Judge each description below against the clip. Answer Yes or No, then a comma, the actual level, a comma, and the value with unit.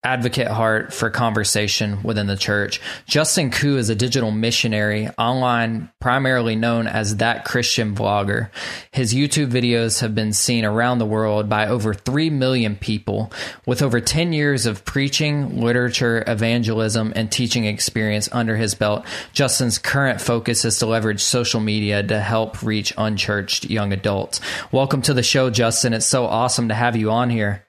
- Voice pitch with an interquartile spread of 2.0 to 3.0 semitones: Yes, narrow, 2.5 semitones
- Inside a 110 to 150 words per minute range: No, average, 165 wpm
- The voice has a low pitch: Yes, low, 115 Hz